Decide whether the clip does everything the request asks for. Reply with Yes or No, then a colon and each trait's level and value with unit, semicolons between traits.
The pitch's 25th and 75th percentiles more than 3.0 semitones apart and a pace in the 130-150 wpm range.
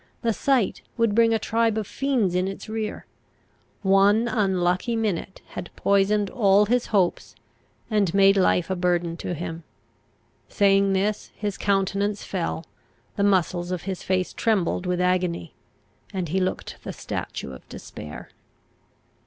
No: average, 2.7 semitones; average, 145 wpm